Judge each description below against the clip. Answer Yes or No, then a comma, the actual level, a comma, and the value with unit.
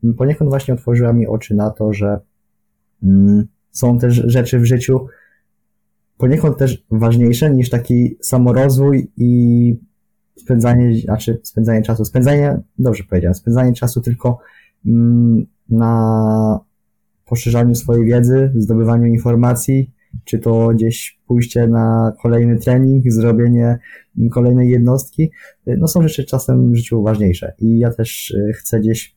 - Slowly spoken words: No, average, 120 wpm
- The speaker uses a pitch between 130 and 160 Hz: No, low, 120 Hz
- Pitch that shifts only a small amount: Yes, narrow, 1.7 semitones